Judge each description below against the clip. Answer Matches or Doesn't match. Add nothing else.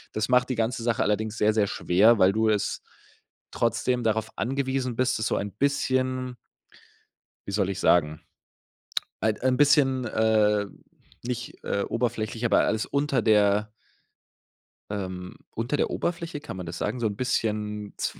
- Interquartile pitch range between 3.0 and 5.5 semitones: Matches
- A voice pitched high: Doesn't match